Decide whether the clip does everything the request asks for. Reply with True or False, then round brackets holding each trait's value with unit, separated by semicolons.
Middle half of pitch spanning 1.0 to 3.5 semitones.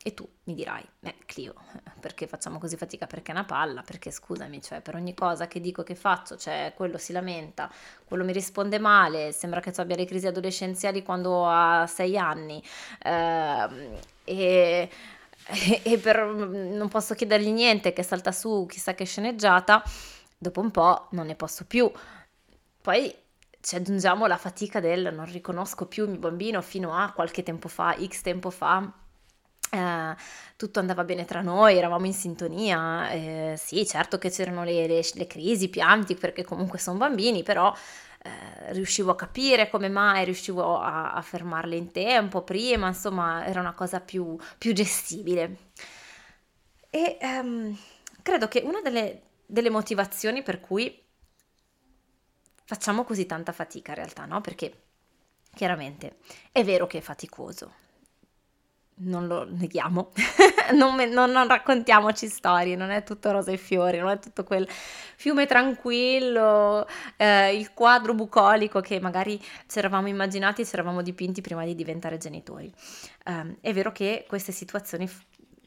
True (3.2 semitones)